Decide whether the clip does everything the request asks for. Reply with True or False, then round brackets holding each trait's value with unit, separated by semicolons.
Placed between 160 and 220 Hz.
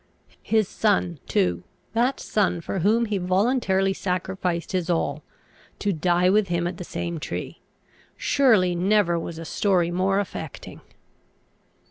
True (185 Hz)